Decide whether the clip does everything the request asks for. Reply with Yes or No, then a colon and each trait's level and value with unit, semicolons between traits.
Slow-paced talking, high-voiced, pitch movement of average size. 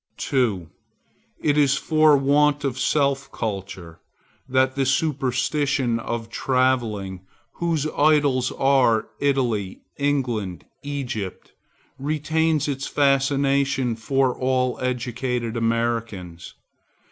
No: slow, 90 wpm; low, 130 Hz; average, 3.5 semitones